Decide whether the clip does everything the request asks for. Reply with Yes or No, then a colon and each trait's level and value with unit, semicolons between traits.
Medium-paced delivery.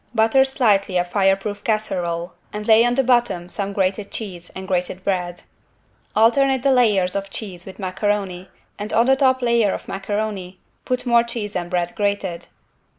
Yes: average, 165 wpm